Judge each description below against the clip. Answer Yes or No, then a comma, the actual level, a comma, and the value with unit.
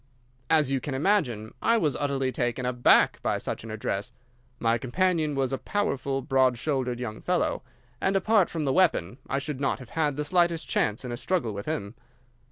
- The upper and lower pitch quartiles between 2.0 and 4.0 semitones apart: No, average, 4.8 semitones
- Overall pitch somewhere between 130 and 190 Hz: Yes, low, 135 Hz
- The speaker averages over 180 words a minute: Yes, average, 190 wpm